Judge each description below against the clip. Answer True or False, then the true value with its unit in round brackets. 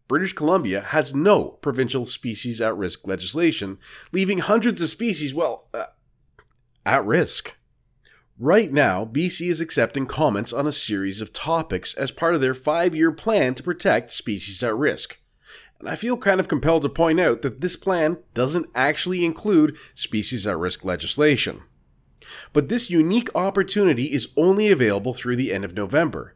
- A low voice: False (150 Hz)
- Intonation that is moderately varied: False (6.8 semitones)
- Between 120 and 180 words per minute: True (160 wpm)